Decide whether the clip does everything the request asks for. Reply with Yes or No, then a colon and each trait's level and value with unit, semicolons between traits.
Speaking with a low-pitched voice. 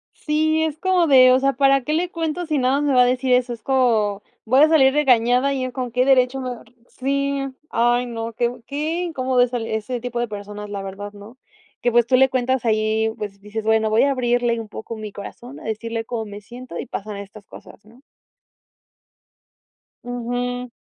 No: high, 245 Hz